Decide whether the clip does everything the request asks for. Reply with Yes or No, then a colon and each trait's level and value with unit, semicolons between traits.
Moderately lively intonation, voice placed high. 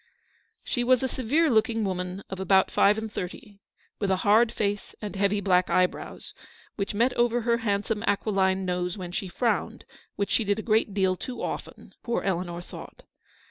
Yes: average, 3.1 semitones; high, 205 Hz